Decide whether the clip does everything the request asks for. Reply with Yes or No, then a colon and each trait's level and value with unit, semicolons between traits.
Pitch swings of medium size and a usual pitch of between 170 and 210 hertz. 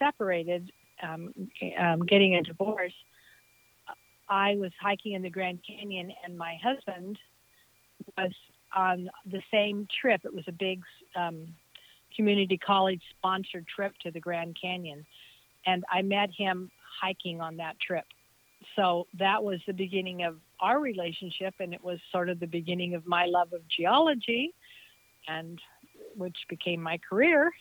No: narrow, 2.3 semitones; medium, 185 Hz